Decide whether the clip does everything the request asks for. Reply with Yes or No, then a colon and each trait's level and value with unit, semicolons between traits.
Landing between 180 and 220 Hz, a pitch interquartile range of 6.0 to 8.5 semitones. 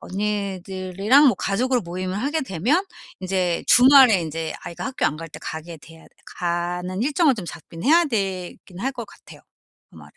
Yes: high, 190 Hz; wide, 6.5 semitones